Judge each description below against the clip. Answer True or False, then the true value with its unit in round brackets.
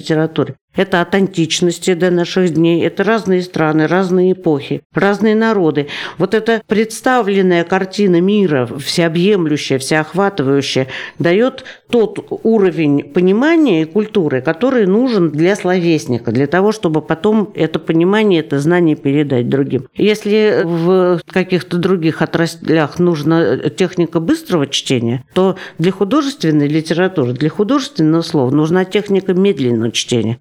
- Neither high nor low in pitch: True (175 Hz)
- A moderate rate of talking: True (120 wpm)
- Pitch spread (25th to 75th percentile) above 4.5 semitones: False (4.2 semitones)